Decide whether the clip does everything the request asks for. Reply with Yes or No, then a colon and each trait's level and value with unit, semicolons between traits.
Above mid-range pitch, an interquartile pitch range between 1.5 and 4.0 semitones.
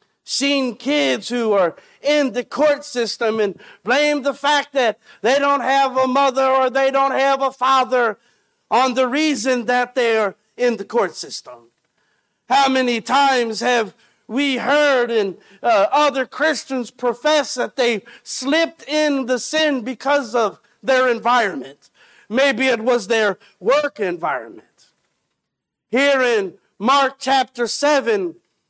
Yes: very high, 260 Hz; average, 2.9 semitones